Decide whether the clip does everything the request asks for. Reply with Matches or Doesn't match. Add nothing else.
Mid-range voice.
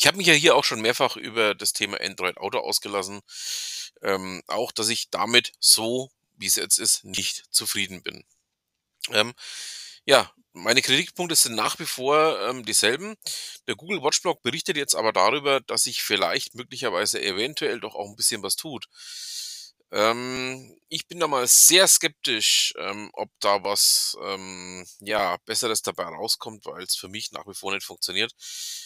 Doesn't match